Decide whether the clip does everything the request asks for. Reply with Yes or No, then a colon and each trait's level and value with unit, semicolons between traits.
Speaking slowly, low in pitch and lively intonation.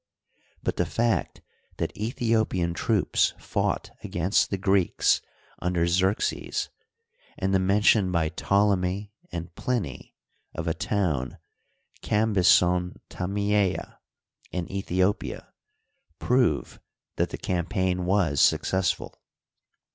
No: slow, 95 wpm; very low, 95 Hz; average, 2.7 semitones